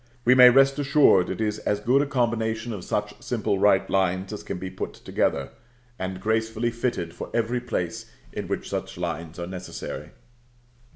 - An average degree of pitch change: Yes, average, 4.6 semitones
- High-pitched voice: No, low, 110 Hz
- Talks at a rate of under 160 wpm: No, average, 175 wpm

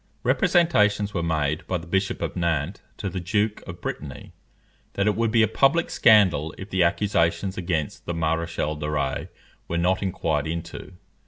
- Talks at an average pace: Yes, average, 170 wpm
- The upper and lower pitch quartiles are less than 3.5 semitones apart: No, average, 4.1 semitones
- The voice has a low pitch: Yes, very low, 85 Hz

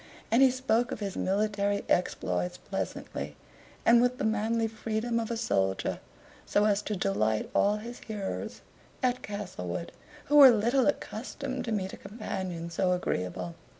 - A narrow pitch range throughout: No, average, 4.3 semitones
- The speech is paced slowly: No, average, 150 wpm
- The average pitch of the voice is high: Yes, high, 210 Hz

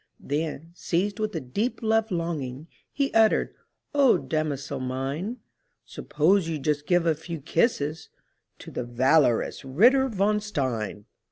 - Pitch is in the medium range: Yes, medium, 160 Hz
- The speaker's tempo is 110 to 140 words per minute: Yes, slow, 135 wpm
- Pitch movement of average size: No, wide, 7.3 semitones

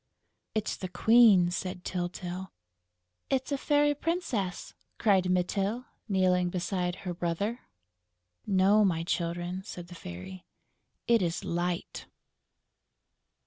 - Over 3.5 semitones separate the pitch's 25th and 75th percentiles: No, average, 3.2 semitones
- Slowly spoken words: Yes, slow, 105 wpm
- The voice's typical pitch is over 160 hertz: Yes, medium, 185 Hz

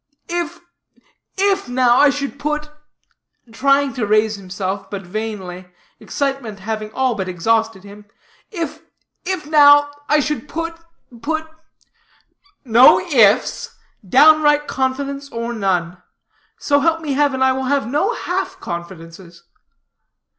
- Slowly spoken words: Yes, slow, 125 wpm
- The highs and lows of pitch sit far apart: Yes, wide, 6.3 semitones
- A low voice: No, very high, 265 Hz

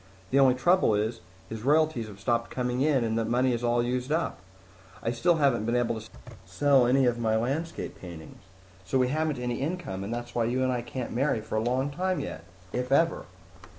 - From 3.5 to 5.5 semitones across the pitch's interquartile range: No, average, 3.1 semitones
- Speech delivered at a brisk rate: Yes, fast, 215 wpm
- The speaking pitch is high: No, low, 125 Hz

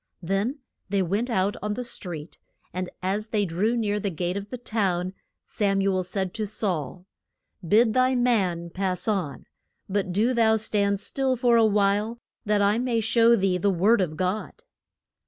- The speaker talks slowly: No, average, 175 wpm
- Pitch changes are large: No, average, 3.3 semitones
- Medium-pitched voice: No, high, 205 Hz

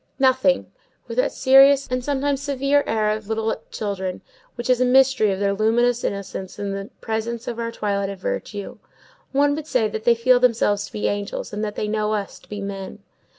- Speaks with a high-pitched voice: Yes, high, 225 Hz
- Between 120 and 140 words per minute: No, average, 200 wpm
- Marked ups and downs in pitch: No, average, 4.1 semitones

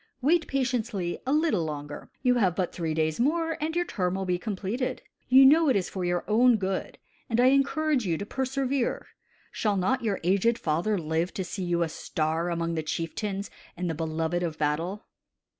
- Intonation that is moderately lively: No, wide, 7.0 semitones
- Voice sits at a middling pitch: No, high, 195 Hz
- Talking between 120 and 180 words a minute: No, average, 190 wpm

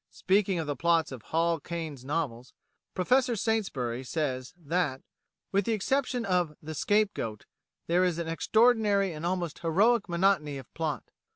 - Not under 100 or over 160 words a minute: Yes, average, 150 wpm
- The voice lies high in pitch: No, medium, 170 Hz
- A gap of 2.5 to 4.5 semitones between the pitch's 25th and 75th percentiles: No, average, 5.0 semitones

